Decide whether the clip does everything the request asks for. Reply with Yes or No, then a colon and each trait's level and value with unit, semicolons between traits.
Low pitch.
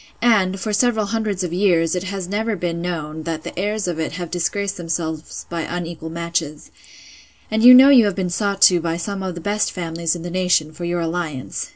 No: medium, 175 Hz